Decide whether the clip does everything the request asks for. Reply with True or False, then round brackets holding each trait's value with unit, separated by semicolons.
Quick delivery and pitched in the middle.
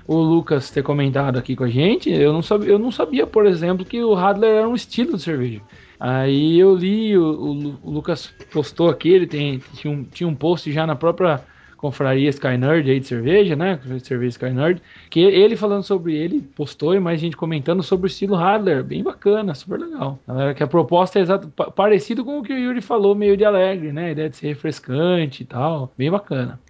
True (215 wpm; 165 Hz)